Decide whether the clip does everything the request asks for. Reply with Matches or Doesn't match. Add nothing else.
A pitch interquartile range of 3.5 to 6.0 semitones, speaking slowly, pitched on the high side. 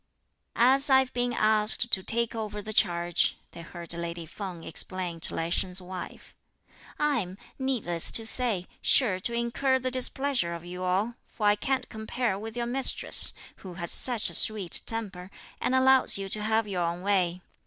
Doesn't match